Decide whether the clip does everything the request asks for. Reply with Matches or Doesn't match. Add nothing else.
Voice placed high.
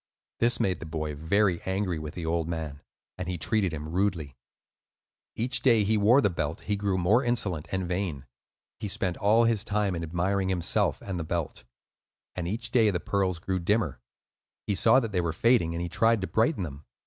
Doesn't match